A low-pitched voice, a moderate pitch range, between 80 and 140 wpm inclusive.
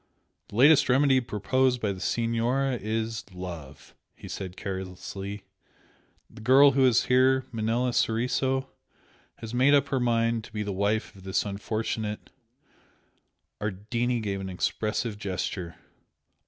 Yes: low, 115 Hz; average, 4.0 semitones; slow, 135 wpm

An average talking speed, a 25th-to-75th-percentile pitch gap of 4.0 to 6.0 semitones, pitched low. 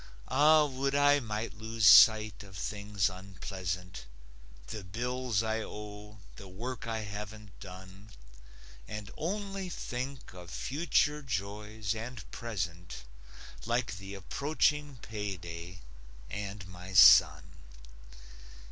No: slow, 105 wpm; average, 4.7 semitones; low, 105 Hz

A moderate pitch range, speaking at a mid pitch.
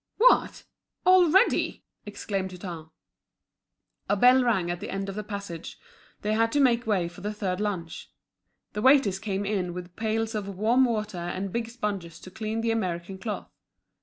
No: average, 3.5 semitones; high, 205 Hz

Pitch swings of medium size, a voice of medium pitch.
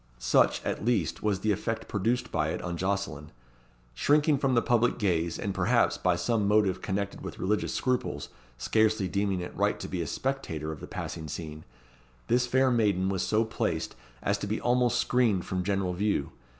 No: average, 4.7 semitones; low, 100 Hz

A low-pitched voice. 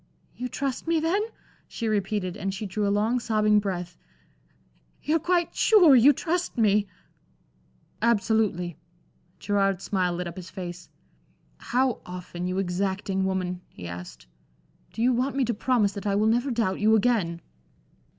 No: high, 210 Hz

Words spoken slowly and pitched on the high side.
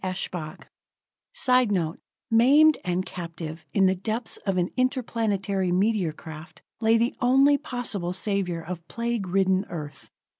Yes: slow, 125 wpm; high, 195 Hz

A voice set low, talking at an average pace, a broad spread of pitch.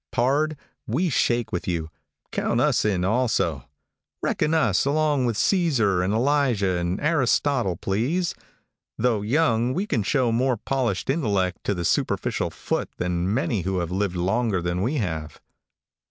Yes: low, 115 Hz; average, 150 wpm; wide, 6.7 semitones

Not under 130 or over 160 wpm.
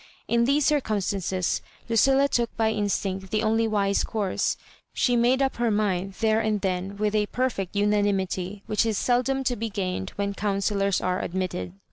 No: average, 170 wpm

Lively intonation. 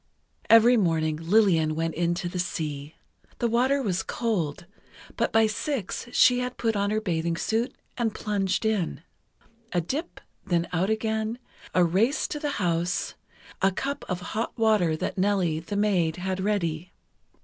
No: average, 4.7 semitones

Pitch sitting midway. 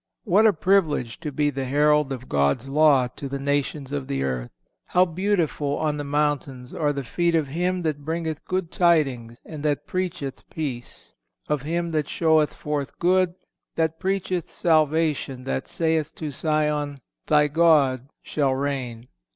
Yes: medium, 150 Hz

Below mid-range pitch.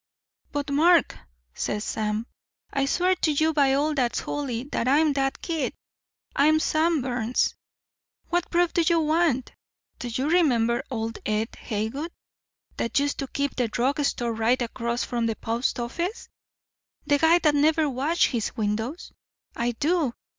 No: very high, 275 Hz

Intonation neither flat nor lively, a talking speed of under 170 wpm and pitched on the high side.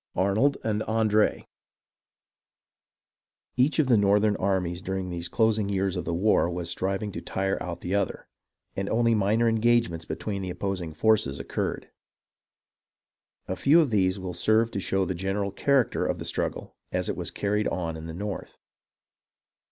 No: average, 3.0 semitones; average, 160 wpm; low, 100 Hz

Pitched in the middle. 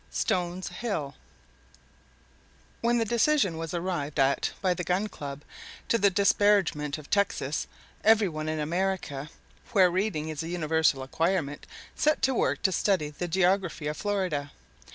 Yes: medium, 180 Hz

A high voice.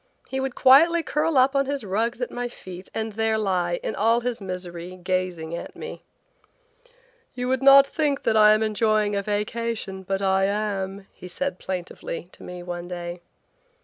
Yes: high, 210 Hz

